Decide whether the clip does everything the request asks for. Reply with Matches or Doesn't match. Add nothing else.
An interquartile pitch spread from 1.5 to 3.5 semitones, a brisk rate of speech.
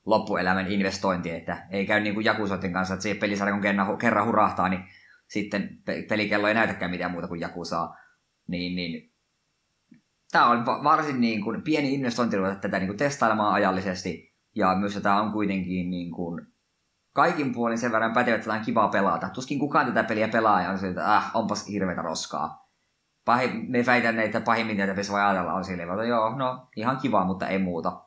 Matches